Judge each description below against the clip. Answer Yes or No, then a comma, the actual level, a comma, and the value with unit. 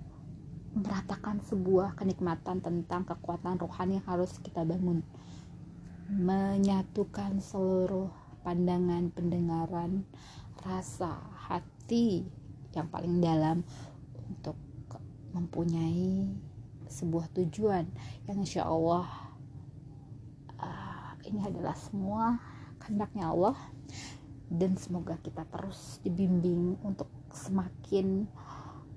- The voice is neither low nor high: Yes, medium, 175 Hz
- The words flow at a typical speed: No, slow, 80 wpm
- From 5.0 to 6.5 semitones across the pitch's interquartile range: Yes, average, 5.3 semitones